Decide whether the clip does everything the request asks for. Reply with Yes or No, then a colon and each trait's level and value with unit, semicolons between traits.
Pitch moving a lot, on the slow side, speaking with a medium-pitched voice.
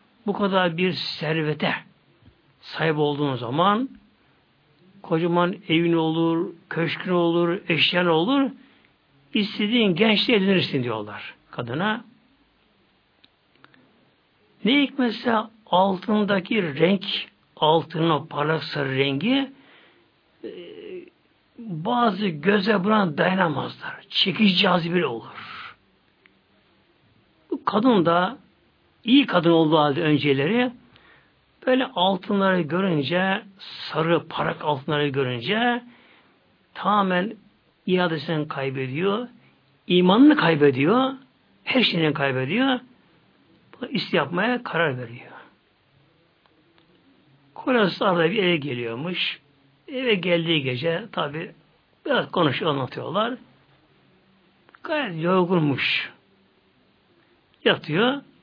Yes: wide, 5.7 semitones; slow, 80 wpm; medium, 180 Hz